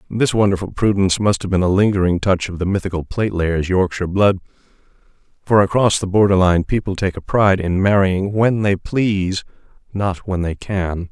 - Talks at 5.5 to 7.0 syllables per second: Yes, 5.6 syllables/s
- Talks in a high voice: No, very low, 95 Hz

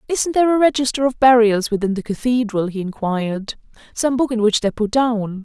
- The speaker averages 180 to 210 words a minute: Yes, average, 200 wpm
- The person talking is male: No, female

